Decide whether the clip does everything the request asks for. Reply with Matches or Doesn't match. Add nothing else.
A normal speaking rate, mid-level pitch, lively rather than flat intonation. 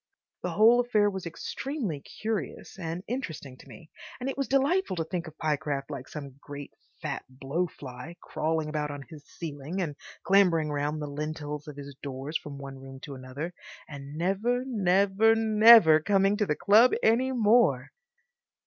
Matches